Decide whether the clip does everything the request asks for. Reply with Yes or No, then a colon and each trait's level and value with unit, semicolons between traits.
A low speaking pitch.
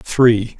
Yes: low, 115 Hz